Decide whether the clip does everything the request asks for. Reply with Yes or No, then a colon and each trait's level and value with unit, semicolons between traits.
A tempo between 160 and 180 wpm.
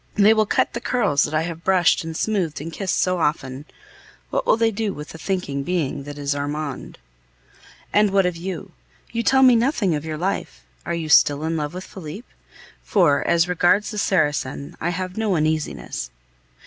No: average, 190 wpm